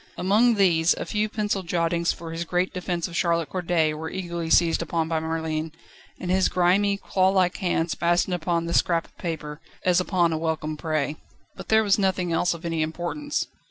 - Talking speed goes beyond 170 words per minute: Yes, average, 190 wpm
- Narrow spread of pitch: Yes, narrow, 2.3 semitones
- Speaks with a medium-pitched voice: Yes, medium, 170 Hz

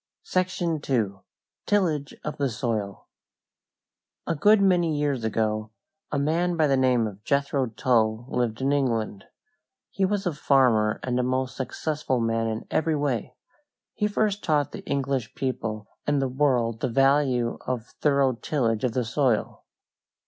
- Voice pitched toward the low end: Yes, low, 130 Hz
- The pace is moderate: Yes, average, 150 wpm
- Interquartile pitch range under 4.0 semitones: No, average, 4.5 semitones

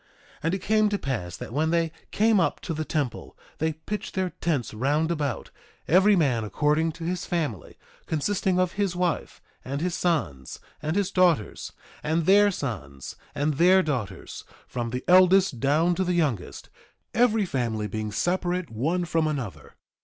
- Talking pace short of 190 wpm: Yes, average, 170 wpm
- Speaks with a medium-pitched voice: Yes, medium, 160 Hz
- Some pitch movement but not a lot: No, wide, 6.1 semitones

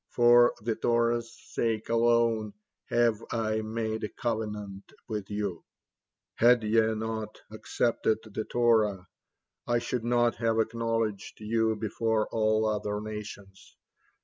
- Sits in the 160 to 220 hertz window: No, low, 110 Hz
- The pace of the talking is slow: Yes, slow, 120 wpm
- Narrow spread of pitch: Yes, narrow, 1.5 semitones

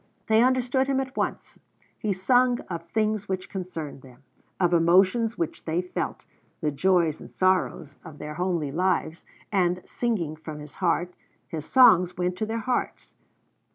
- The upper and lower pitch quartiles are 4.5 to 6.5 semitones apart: Yes, average, 5.0 semitones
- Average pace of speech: Yes, average, 155 wpm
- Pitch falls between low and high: Yes, medium, 180 Hz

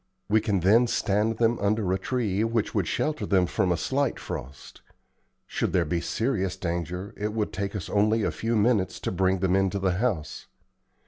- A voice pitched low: Yes, low, 100 Hz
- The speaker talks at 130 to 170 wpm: No, average, 190 wpm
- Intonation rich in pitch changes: No, average, 3.3 semitones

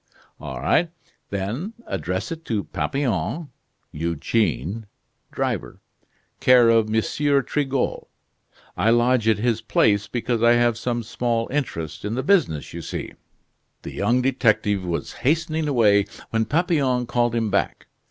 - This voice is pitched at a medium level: No, low, 115 Hz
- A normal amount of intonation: Yes, average, 4.2 semitones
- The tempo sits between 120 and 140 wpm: Yes, slow, 135 wpm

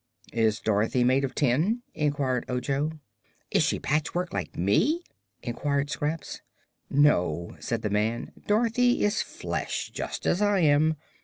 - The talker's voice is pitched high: No, medium, 145 Hz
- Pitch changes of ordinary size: No, wide, 5.8 semitones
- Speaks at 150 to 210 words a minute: No, slow, 135 wpm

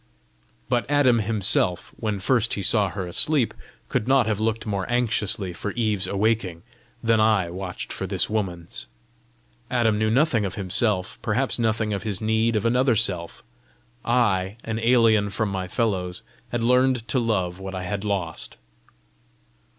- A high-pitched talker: No, low, 110 Hz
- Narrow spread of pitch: No, average, 3.4 semitones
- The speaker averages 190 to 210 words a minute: No, average, 155 wpm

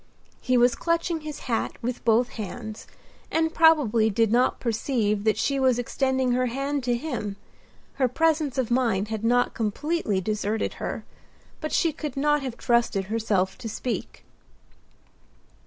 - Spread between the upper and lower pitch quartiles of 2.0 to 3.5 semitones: No, average, 4.1 semitones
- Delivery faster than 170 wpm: No, average, 150 wpm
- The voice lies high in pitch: Yes, high, 245 Hz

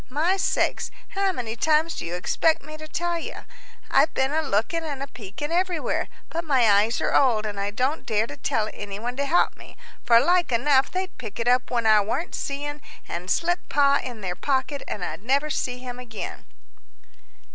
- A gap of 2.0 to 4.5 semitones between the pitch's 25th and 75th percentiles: No, wide, 5.6 semitones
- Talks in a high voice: Yes, very high, 265 Hz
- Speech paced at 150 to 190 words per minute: No, average, 200 wpm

